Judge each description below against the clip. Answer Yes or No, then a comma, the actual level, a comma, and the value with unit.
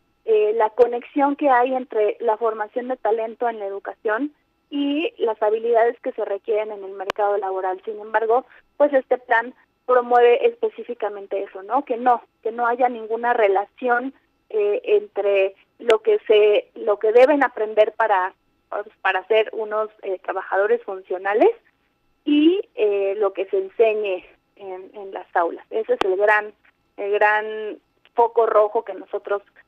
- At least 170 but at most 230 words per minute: No, average, 150 wpm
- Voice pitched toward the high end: Yes, high, 225 Hz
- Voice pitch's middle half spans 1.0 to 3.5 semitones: No, average, 4.3 semitones